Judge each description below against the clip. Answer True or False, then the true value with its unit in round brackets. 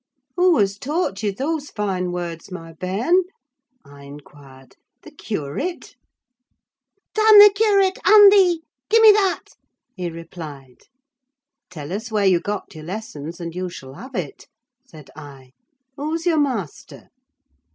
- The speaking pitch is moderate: False (195 Hz)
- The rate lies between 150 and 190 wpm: False (135 wpm)